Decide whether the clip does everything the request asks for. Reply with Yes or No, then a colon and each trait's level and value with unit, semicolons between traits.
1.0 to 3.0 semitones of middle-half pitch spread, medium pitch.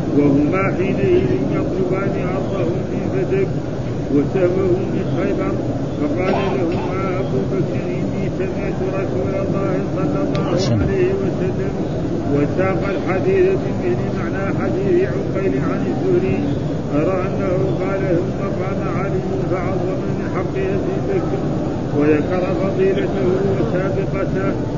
No: average, 4.3 semitones; medium, 175 Hz